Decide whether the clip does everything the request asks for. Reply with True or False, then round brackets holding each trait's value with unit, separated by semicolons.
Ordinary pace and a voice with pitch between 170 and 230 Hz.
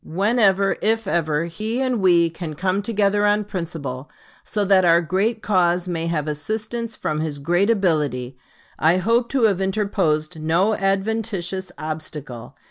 True (145 wpm; 185 Hz)